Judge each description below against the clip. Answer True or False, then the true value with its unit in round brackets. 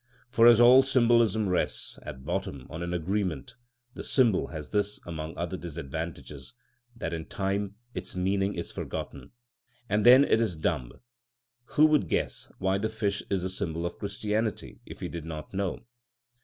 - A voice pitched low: True (95 Hz)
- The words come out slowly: False (165 wpm)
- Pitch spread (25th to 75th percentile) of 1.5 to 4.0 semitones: False (4.7 semitones)